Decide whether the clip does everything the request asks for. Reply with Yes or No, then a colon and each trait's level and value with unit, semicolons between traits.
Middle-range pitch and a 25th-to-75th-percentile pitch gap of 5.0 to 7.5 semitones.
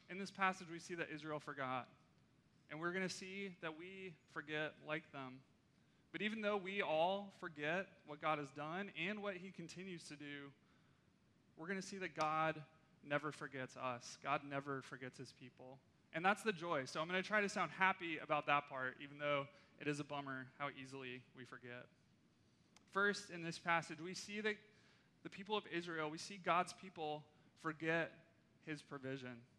No: medium, 155 Hz; average, 4.6 semitones